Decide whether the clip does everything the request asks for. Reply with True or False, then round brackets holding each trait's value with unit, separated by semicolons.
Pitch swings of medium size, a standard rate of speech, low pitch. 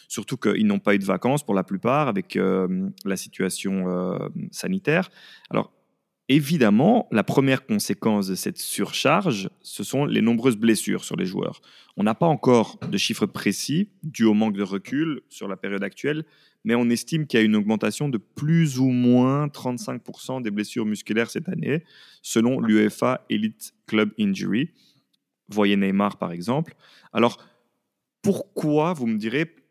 False (6.8 semitones; 160 wpm; 120 Hz)